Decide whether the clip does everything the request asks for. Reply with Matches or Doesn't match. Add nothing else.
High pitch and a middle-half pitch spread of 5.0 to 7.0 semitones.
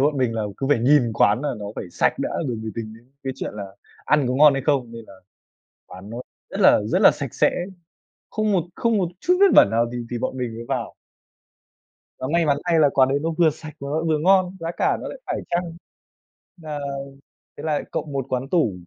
Doesn't match